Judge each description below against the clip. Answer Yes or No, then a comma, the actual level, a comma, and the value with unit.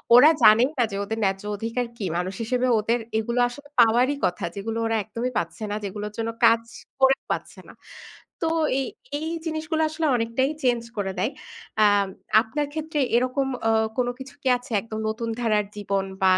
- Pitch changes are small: No, average, 3.4 semitones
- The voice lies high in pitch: Yes, high, 230 Hz